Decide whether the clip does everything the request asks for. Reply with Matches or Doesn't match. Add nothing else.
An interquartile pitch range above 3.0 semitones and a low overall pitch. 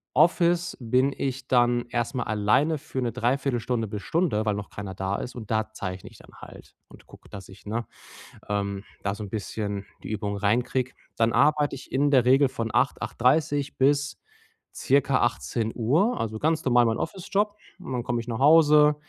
Matches